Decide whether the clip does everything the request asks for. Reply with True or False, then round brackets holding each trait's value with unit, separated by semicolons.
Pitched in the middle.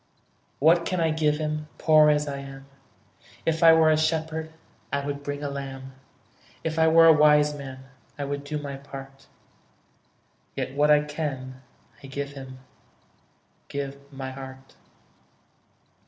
True (145 Hz)